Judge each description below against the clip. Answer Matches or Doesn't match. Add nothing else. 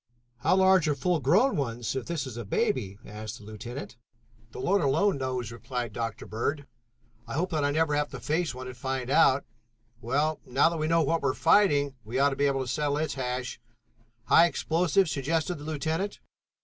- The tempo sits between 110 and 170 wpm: Doesn't match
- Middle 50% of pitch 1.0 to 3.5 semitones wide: Doesn't match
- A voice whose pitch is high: Doesn't match